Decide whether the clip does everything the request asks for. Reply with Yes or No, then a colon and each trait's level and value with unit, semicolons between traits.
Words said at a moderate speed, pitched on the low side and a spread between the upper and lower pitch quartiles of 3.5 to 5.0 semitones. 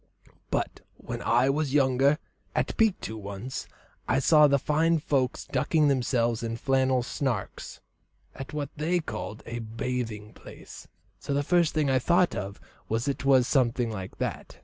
Yes: average, 160 wpm; low, 130 Hz; average, 4.1 semitones